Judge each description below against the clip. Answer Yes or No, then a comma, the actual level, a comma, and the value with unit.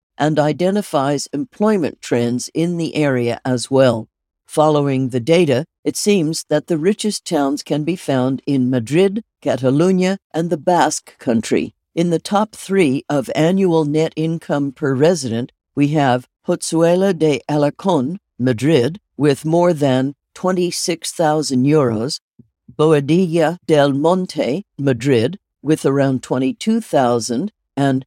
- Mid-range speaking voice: Yes, medium, 155 Hz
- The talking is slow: Yes, slow, 125 wpm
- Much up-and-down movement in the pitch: No, average, 4.4 semitones